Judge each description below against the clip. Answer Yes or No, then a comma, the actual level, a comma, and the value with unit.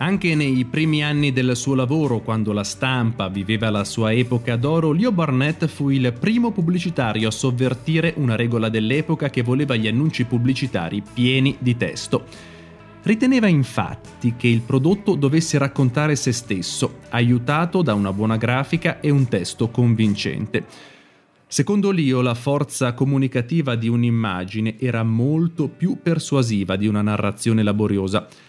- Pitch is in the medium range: No, low, 130 Hz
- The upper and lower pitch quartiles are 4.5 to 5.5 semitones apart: Yes, average, 4.9 semitones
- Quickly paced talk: No, average, 140 wpm